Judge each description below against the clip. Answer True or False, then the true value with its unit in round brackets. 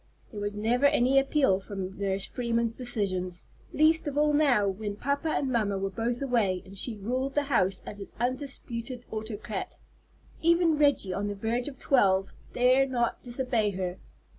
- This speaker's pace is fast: False (165 wpm)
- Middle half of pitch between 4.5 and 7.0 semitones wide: True (5.1 semitones)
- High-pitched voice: True (235 Hz)